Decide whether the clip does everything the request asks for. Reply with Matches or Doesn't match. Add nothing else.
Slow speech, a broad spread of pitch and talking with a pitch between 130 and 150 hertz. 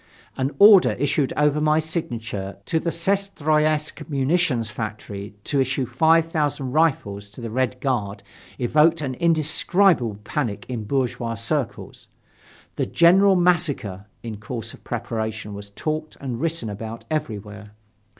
Matches